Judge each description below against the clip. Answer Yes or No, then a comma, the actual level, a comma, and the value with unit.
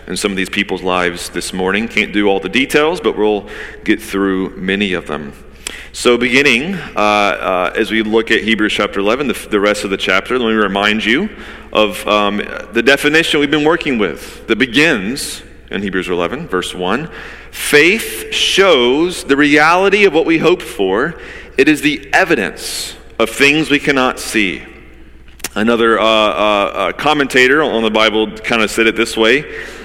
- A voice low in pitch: Yes, low, 110 Hz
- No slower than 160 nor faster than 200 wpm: Yes, average, 175 wpm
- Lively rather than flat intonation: Yes, wide, 6.1 semitones